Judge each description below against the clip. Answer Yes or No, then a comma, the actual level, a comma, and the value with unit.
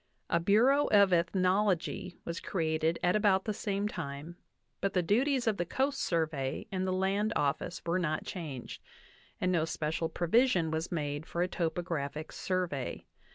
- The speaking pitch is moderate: Yes, medium, 175 Hz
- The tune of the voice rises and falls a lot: No, average, 3.7 semitones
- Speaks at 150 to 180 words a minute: Yes, average, 160 wpm